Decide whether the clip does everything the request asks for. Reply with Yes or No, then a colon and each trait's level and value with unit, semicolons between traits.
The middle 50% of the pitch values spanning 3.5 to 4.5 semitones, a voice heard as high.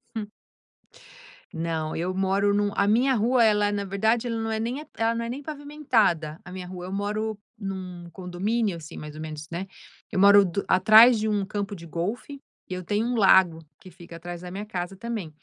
Yes: average, 3.9 semitones; high, 200 Hz